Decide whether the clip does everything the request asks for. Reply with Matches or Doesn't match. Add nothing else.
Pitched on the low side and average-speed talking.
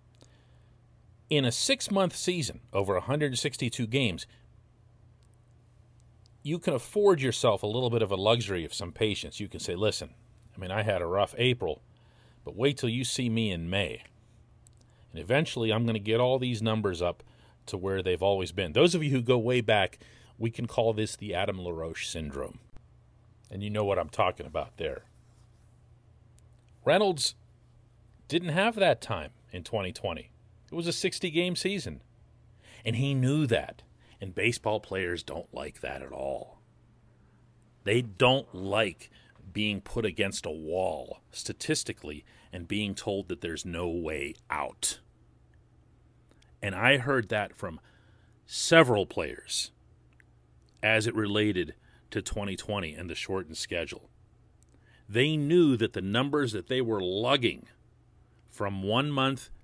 Matches